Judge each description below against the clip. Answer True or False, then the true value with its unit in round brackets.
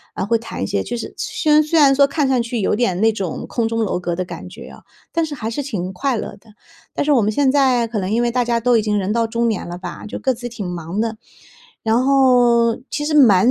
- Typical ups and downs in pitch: True (4.0 semitones)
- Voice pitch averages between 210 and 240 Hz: True (230 Hz)